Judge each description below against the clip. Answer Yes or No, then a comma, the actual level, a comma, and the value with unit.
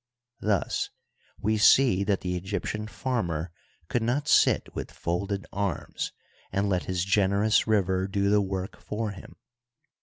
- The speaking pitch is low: Yes, low, 100 Hz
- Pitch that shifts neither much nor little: No, narrow, 2.3 semitones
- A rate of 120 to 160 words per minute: Yes, average, 140 wpm